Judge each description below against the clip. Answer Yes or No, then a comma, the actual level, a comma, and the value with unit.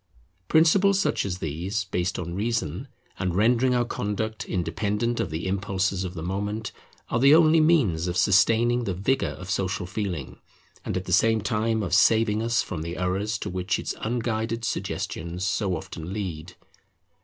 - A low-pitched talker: Yes, low, 100 Hz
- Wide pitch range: No, average, 4.0 semitones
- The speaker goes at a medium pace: Yes, average, 165 wpm